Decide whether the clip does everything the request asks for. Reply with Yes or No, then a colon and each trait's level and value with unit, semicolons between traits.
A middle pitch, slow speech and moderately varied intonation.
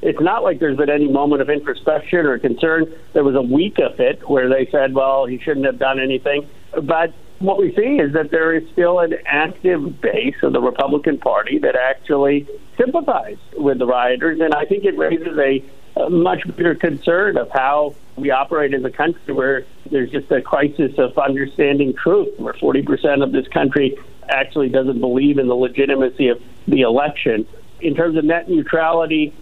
No: medium, 145 Hz; average, 185 wpm; average, 3.5 semitones